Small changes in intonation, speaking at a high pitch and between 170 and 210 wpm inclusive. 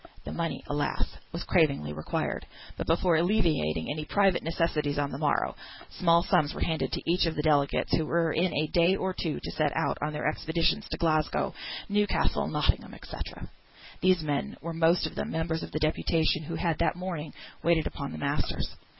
No: narrow, 2.2 semitones; medium, 160 Hz; average, 190 wpm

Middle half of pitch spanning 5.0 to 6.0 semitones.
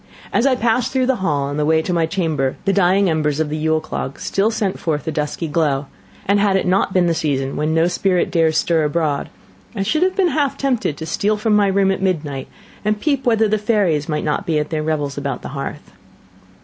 Yes: average, 5.3 semitones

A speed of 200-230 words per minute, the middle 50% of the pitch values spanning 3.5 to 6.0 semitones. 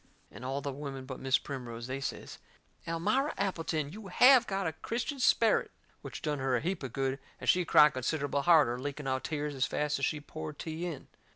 Yes: fast, 205 wpm; average, 4.0 semitones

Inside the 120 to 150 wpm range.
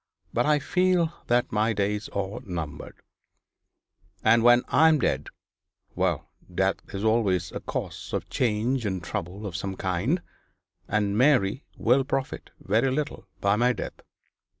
Yes: average, 145 wpm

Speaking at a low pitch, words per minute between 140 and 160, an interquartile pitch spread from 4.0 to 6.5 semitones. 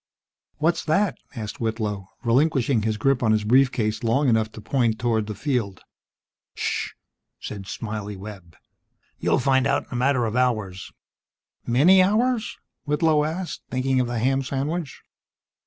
Yes: low, 125 Hz; average, 150 wpm; average, 4.6 semitones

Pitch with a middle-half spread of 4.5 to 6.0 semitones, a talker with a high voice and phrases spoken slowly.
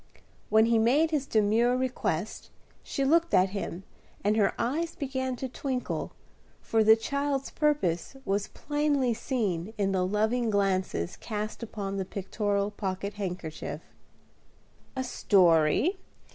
Yes: average, 4.9 semitones; high, 220 Hz; slow, 130 wpm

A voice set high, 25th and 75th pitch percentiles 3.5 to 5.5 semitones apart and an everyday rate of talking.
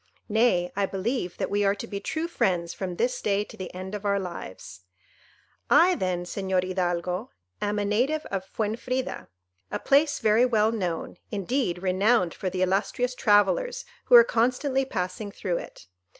Yes: high, 205 Hz; average, 5.0 semitones; average, 165 wpm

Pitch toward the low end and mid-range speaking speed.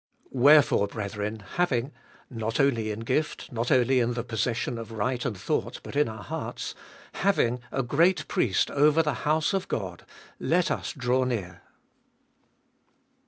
Yes: low, 120 Hz; average, 155 wpm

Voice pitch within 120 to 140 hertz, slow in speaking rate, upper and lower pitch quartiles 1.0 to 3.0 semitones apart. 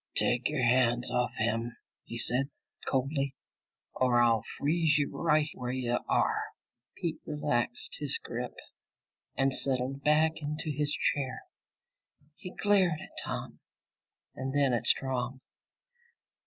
No: low, 135 Hz; slow, 125 wpm; average, 3.6 semitones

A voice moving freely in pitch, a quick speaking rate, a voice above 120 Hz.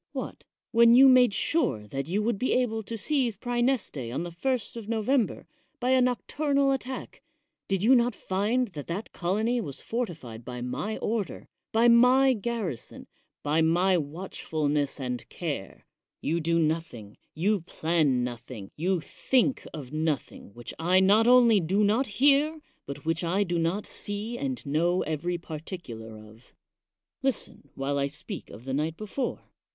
No: wide, 7.9 semitones; average, 160 wpm; medium, 185 Hz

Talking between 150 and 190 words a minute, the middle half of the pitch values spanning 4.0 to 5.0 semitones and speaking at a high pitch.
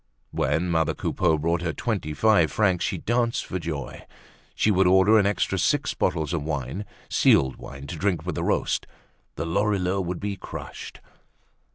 No: average, 170 wpm; average, 4.3 semitones; very low, 90 Hz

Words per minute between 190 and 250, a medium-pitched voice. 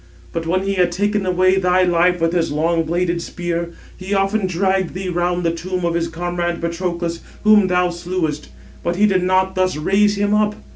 Yes: average, 195 wpm; medium, 180 Hz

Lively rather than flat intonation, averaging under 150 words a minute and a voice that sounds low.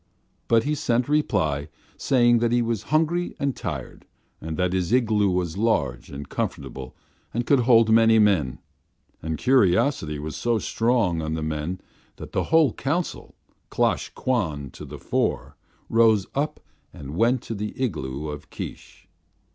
No: wide, 7.4 semitones; average, 155 wpm; low, 105 Hz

